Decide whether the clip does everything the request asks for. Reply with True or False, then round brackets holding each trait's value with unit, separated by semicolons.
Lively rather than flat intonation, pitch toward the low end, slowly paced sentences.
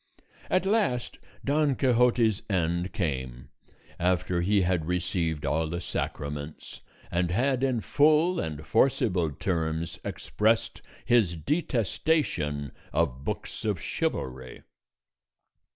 True (7.6 semitones; 90 Hz; 105 wpm)